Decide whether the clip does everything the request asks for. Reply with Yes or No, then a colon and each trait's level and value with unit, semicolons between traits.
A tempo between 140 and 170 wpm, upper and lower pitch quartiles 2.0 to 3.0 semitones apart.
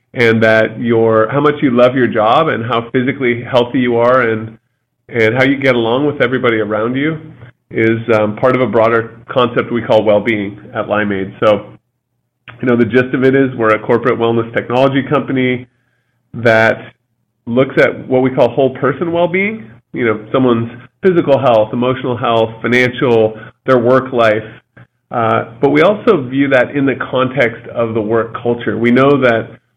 No: average, 180 wpm; narrow, 2.4 semitones